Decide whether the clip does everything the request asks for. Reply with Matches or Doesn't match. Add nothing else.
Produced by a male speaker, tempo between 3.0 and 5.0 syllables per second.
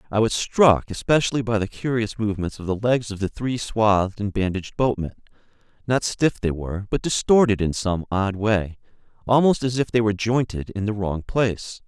Doesn't match